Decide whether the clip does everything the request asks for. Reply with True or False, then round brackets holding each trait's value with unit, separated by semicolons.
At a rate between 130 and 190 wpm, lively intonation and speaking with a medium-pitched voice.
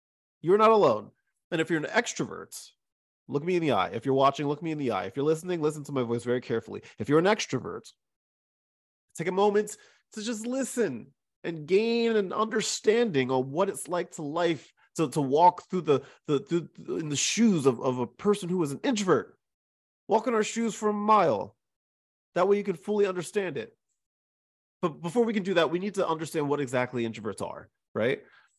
False (205 wpm; 6.5 semitones; 170 Hz)